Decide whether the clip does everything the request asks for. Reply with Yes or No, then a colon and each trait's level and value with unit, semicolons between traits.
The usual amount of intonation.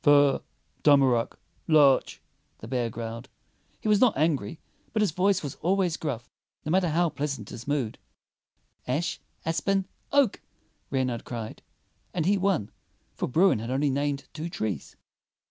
No: wide, 5.8 semitones